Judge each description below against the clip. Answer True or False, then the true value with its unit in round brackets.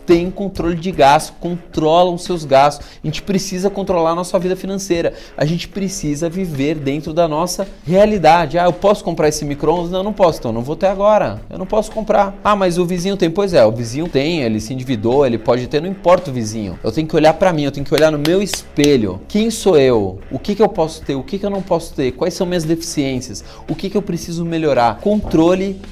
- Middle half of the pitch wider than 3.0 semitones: True (4.3 semitones)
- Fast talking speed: True (240 wpm)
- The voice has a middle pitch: True (175 Hz)